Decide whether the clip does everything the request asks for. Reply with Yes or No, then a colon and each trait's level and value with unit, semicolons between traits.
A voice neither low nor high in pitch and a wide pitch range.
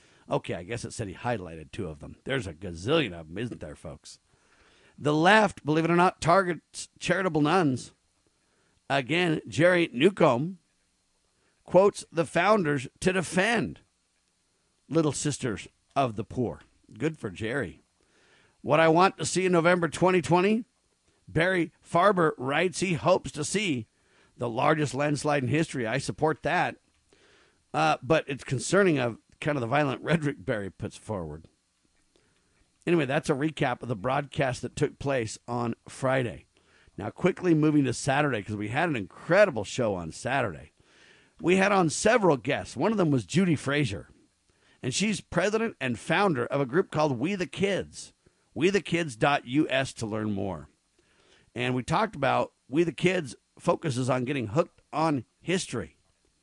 Yes: medium, 150 Hz; wide, 6.0 semitones